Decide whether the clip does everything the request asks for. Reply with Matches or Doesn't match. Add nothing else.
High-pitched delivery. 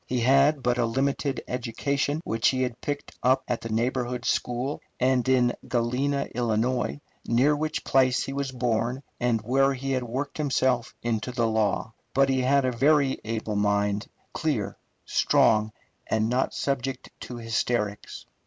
Doesn't match